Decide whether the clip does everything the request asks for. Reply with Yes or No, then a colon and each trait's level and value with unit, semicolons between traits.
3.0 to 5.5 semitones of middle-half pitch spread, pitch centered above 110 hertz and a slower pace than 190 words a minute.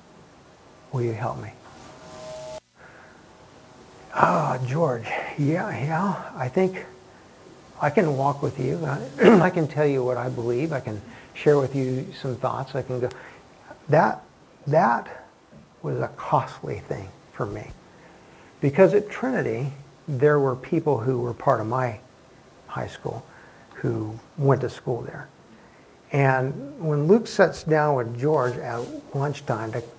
Yes: average, 3.6 semitones; low, 135 Hz; average, 140 wpm